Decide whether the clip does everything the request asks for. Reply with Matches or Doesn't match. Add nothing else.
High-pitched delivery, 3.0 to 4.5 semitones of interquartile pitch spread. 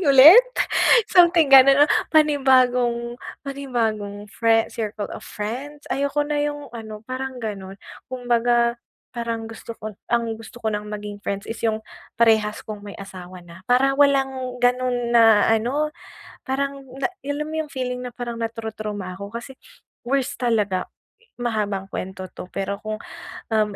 Matches